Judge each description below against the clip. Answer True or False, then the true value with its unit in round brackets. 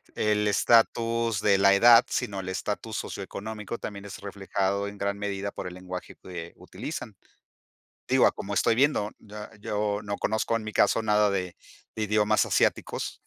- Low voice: True (105 Hz)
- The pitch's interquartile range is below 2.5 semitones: True (1.7 semitones)